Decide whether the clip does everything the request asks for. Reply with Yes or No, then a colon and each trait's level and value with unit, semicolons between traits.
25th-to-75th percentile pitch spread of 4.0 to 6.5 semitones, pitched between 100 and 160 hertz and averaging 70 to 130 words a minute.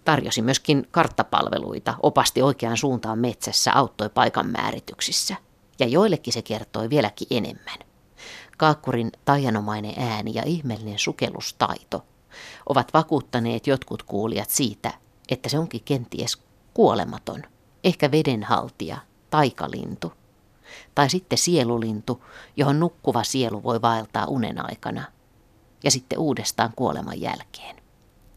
Yes: average, 4.4 semitones; low, 125 Hz; average, 105 wpm